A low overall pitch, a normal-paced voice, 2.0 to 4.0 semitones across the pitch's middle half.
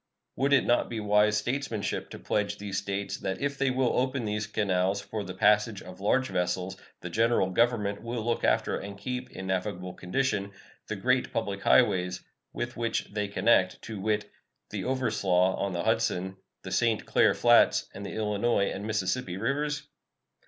Yes: low, 105 Hz; average, 175 wpm; average, 3.7 semitones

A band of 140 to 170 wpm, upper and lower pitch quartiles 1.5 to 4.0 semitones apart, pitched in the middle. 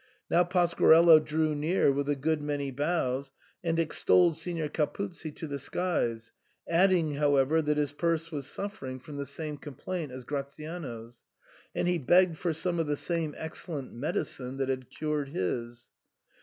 Yes: average, 155 wpm; average, 3.3 semitones; medium, 150 Hz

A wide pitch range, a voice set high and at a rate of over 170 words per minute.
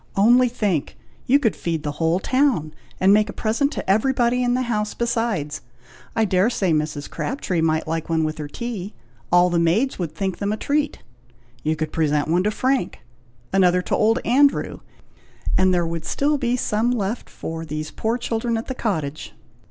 Yes: wide, 6.6 semitones; high, 200 Hz; average, 185 wpm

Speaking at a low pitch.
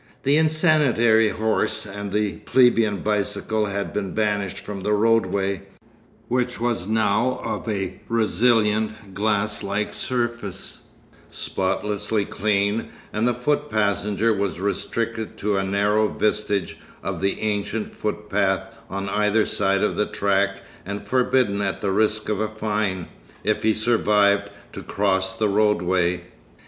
Yes: low, 105 Hz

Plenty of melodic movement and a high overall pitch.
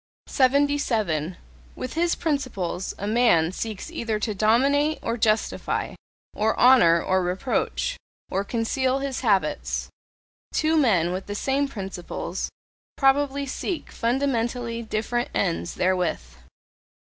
Yes: wide, 6.1 semitones; high, 230 Hz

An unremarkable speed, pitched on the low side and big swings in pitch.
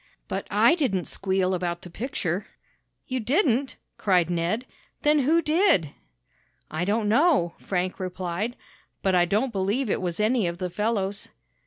No: average, 150 wpm; high, 200 Hz; wide, 6.0 semitones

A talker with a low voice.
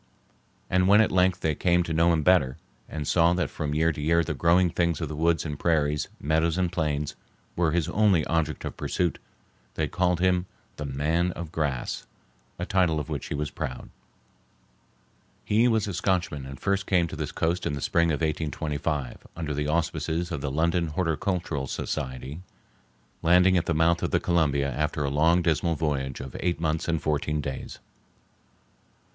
Yes: very low, 80 Hz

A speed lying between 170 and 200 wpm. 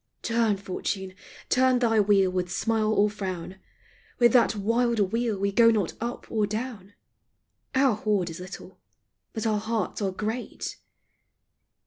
No: average, 140 wpm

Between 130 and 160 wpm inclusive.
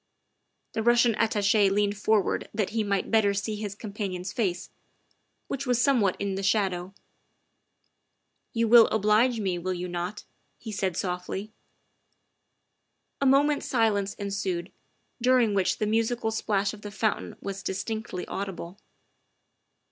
Yes: average, 140 wpm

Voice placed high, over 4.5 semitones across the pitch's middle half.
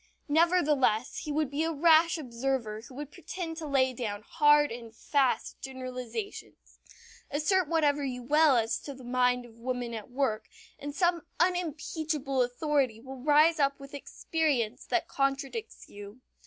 No: very high, 275 Hz; average, 3.9 semitones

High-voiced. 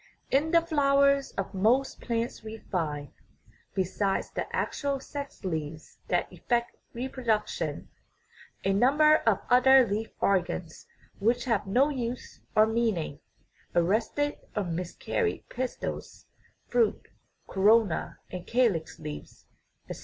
Yes: high, 225 Hz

